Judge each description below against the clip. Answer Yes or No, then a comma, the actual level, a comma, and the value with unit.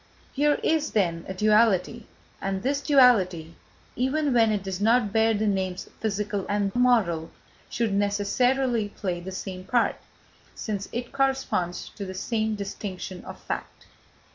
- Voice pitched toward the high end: Yes, high, 210 Hz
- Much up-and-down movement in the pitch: No, average, 4.1 semitones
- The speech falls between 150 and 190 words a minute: No, average, 140 wpm